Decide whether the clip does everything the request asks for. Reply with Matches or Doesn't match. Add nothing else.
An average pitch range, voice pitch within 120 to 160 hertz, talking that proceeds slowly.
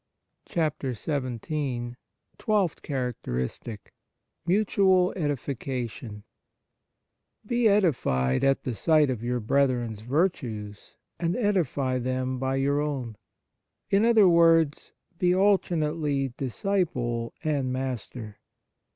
Doesn't match